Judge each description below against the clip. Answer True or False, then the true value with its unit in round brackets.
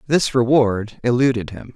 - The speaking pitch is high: False (120 Hz)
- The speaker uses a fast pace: False (135 wpm)